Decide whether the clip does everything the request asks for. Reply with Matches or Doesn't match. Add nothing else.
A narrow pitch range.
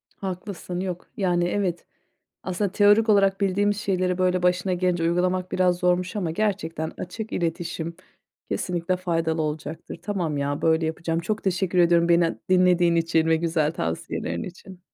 Matches